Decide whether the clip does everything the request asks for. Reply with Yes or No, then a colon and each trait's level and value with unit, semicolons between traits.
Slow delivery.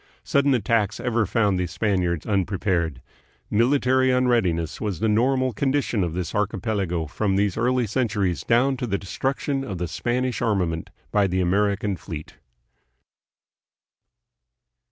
Yes: slow, 130 wpm